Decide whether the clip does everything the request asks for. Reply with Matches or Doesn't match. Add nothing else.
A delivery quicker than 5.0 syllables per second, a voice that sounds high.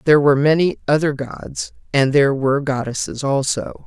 Doesn't match